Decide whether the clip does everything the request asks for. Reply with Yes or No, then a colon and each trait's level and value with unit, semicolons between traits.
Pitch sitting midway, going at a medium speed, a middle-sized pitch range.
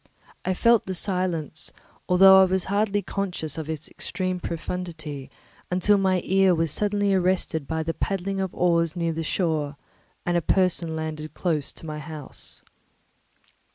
Yes: medium, 175 Hz; average, 155 wpm; average, 3.1 semitones